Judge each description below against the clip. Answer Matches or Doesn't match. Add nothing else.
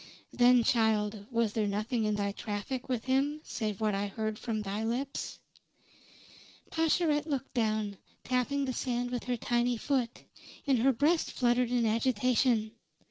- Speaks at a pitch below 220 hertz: Doesn't match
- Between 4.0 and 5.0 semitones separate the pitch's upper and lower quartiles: Doesn't match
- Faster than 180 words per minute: Doesn't match